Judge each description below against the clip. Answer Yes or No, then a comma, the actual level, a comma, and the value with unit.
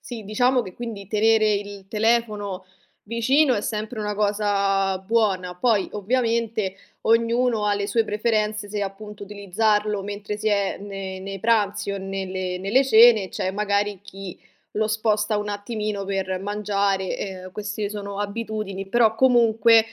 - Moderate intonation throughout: No, narrow, 2.0 semitones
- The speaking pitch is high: Yes, high, 210 Hz